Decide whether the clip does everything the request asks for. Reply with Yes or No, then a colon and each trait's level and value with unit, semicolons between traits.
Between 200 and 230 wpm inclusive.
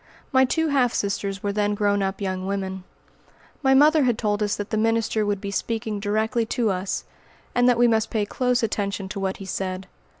Yes: fast, 205 wpm